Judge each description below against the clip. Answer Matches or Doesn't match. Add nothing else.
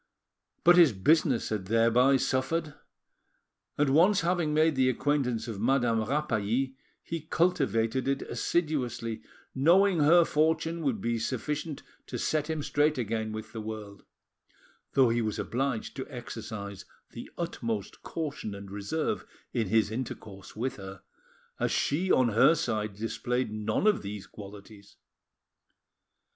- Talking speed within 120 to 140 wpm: Matches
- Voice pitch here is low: Matches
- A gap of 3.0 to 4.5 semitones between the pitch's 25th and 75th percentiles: Doesn't match